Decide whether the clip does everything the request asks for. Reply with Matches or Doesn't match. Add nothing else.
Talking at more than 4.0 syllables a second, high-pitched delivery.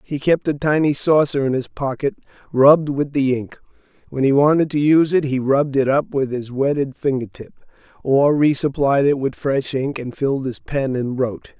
Doesn't match